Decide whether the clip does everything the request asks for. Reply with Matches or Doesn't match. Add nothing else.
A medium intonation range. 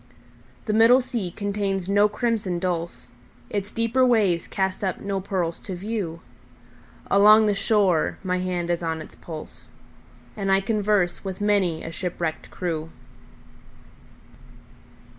Matches